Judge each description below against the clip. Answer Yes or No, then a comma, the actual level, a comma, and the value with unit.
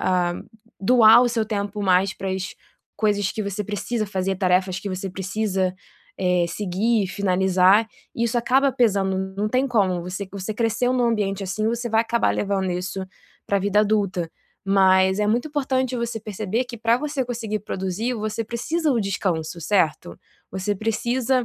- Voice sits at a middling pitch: No, high, 205 Hz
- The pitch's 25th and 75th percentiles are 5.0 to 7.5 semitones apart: No, average, 3.5 semitones